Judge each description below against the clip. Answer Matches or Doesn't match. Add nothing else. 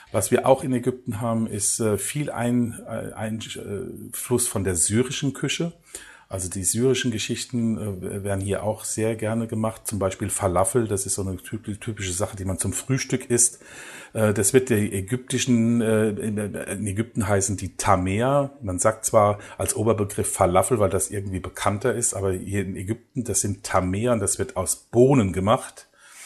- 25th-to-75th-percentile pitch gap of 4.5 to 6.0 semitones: Doesn't match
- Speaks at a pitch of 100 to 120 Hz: Matches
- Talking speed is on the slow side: Doesn't match